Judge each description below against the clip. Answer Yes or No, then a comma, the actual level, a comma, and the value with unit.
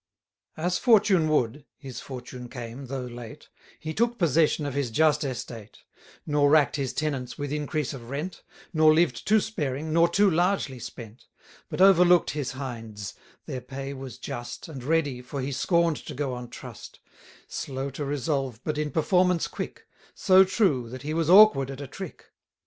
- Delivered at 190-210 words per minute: No, average, 170 wpm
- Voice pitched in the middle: Yes, medium, 145 Hz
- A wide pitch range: No, average, 4.2 semitones